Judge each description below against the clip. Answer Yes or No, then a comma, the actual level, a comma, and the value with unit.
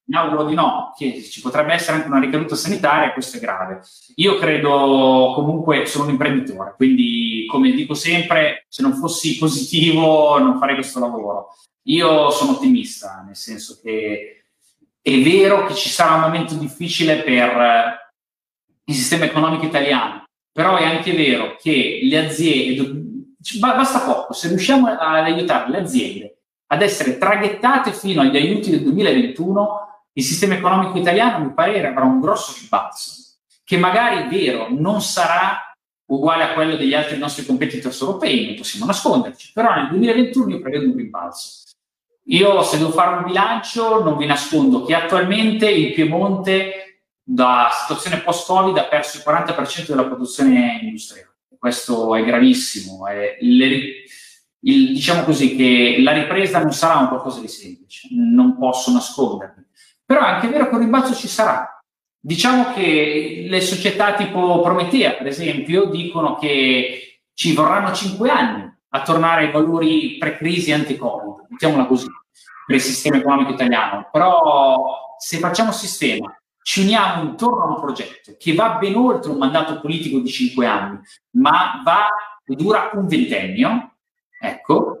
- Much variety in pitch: Yes, wide, 8.2 semitones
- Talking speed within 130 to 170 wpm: Yes, average, 150 wpm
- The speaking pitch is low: No, medium, 165 Hz